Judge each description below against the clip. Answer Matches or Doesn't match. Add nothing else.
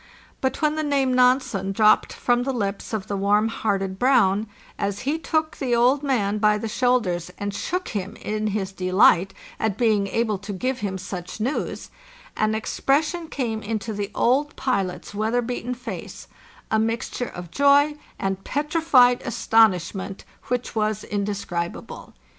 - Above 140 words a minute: Matches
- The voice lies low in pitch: Doesn't match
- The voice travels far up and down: Doesn't match